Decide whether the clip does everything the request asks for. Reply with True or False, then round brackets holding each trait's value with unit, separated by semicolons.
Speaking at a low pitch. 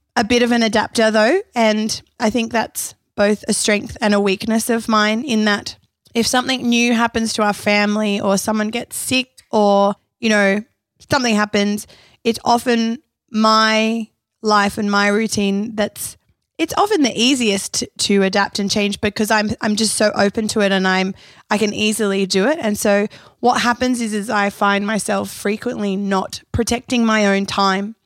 False (215 Hz)